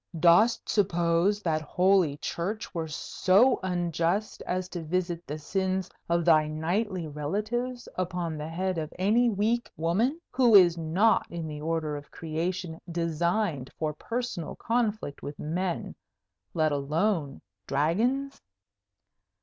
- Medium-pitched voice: Yes, medium, 175 Hz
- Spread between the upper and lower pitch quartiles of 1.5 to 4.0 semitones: No, average, 4.4 semitones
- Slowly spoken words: Yes, slow, 125 wpm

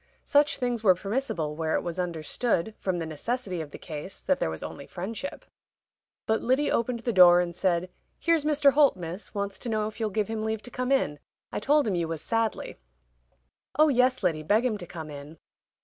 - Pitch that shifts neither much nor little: No, wide, 6.5 semitones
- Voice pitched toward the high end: Yes, high, 205 Hz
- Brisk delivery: Yes, fast, 210 wpm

